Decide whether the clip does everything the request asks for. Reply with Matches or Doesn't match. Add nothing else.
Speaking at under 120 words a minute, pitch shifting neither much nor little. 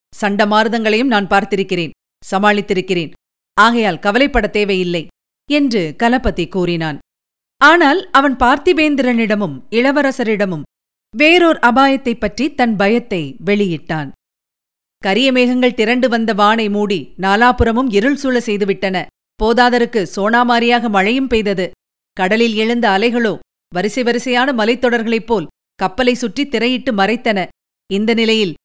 Matches